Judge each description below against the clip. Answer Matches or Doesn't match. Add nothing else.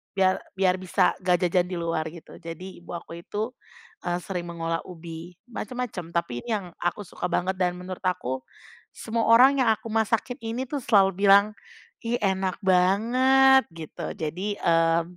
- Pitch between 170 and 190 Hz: Matches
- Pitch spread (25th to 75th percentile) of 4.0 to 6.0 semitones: Matches